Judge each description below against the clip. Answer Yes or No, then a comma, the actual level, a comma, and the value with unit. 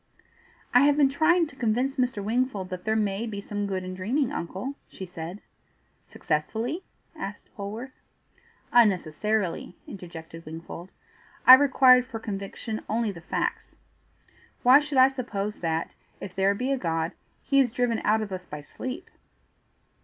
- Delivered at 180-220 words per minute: No, average, 150 wpm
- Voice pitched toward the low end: No, high, 215 Hz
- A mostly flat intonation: No, wide, 5.5 semitones